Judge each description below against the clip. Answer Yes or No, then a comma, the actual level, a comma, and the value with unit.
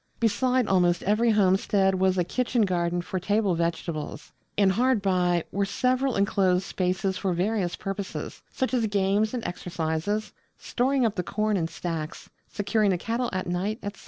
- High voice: Yes, high, 195 Hz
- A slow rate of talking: No, average, 160 wpm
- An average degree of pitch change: Yes, average, 3.3 semitones